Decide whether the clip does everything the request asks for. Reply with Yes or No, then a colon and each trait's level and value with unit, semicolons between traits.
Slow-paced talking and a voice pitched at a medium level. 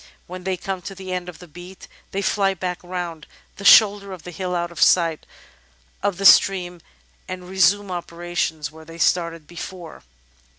No: average, 175 wpm; medium, 180 Hz